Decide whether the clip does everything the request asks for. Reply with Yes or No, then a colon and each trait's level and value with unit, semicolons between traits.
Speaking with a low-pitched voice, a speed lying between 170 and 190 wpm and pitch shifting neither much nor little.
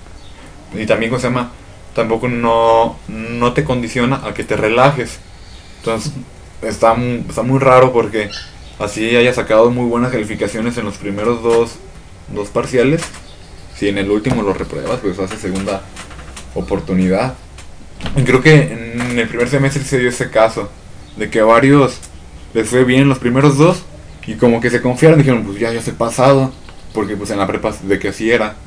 Yes: low, 115 Hz; average, 175 wpm; average, 3.8 semitones